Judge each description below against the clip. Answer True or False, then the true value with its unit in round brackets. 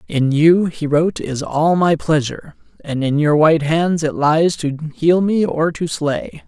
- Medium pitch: True (155 Hz)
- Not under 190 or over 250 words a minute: False (175 wpm)